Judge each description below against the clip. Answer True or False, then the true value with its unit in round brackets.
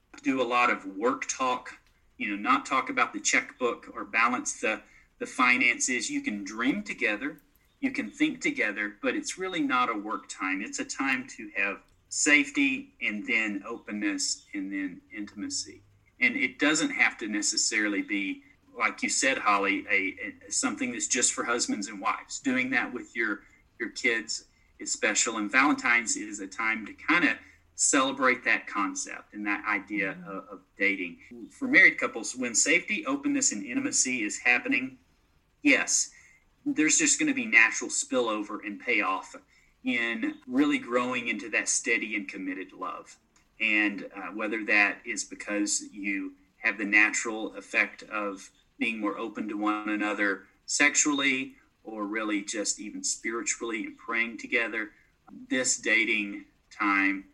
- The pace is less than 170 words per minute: True (155 wpm)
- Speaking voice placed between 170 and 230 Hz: False (275 Hz)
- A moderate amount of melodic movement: False (7.7 semitones)